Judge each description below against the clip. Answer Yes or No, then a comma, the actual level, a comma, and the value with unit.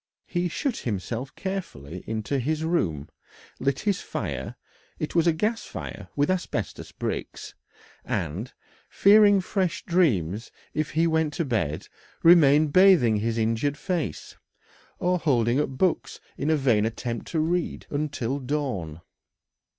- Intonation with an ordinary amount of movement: No, wide, 7.2 semitones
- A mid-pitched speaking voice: Yes, medium, 145 Hz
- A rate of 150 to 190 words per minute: No, slow, 135 wpm